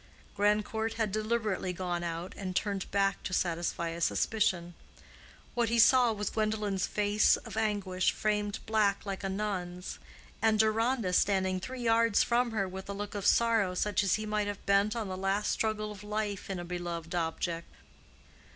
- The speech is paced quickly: No, average, 170 wpm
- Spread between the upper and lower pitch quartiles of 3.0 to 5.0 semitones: No, narrow, 2.6 semitones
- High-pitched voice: Yes, high, 205 Hz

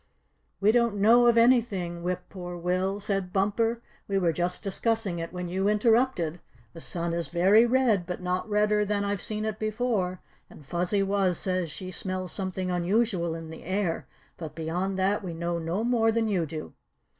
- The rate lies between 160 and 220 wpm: Yes, average, 180 wpm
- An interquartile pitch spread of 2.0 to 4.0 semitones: Yes, average, 3.3 semitones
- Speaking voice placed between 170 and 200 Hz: Yes, high, 190 Hz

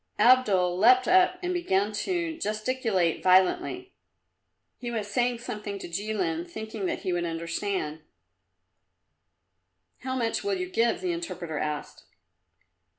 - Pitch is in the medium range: No, high, 215 Hz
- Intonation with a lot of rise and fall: Yes, wide, 6.0 semitones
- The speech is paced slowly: Yes, slow, 125 wpm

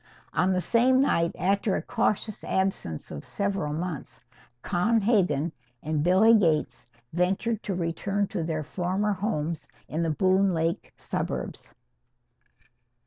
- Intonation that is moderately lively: Yes, average, 3.6 semitones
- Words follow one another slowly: Yes, slow, 130 wpm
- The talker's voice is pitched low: No, medium, 185 Hz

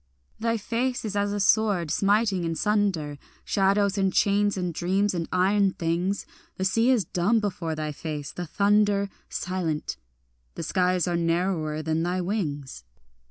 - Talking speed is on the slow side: No, average, 155 wpm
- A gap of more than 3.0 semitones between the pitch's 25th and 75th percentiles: Yes, average, 3.5 semitones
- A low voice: No, medium, 185 Hz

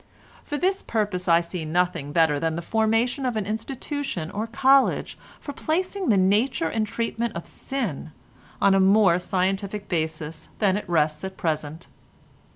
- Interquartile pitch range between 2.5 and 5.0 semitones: No, wide, 5.4 semitones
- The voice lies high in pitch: Yes, high, 195 Hz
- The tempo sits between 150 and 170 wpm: Yes, average, 160 wpm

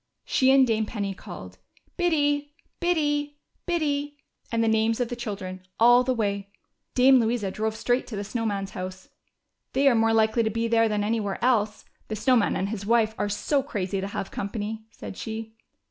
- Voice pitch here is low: No, high, 225 Hz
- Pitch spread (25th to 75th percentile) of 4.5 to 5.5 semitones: No, average, 3.9 semitones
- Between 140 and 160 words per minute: No, average, 190 wpm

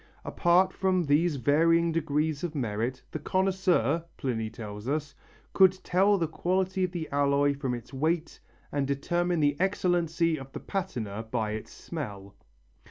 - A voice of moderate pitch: Yes, medium, 155 Hz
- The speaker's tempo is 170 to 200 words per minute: No, average, 150 wpm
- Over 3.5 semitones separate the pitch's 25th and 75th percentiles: Yes, average, 4.8 semitones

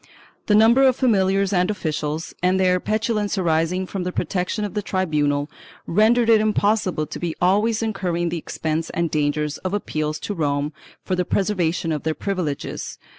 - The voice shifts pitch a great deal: No, average, 4.6 semitones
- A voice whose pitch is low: No, medium, 185 Hz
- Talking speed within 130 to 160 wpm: No, average, 170 wpm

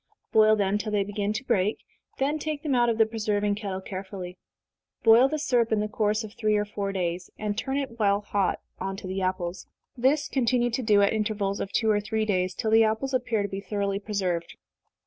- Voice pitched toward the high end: Yes, high, 210 Hz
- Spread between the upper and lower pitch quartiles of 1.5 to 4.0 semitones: Yes, narrow, 2.5 semitones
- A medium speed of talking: No, fast, 220 wpm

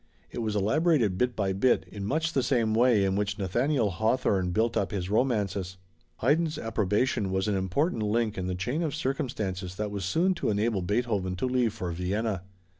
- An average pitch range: Yes, average, 4.6 semitones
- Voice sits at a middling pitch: No, low, 105 Hz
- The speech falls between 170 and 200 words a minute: Yes, average, 190 wpm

